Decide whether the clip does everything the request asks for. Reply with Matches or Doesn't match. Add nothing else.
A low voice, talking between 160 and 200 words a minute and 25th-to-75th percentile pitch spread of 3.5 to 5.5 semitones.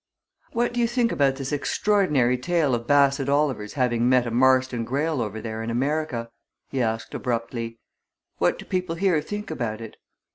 Matches